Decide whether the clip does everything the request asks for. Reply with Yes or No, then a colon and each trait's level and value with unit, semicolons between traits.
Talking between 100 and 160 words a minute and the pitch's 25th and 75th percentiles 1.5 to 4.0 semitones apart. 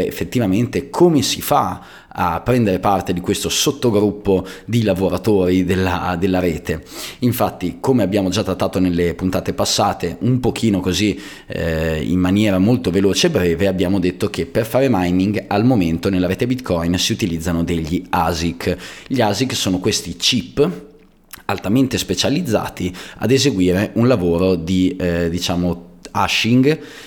Yes: average, 140 wpm; average, 2.8 semitones